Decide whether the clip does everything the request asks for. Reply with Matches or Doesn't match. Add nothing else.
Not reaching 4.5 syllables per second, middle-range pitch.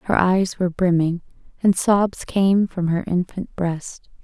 Matches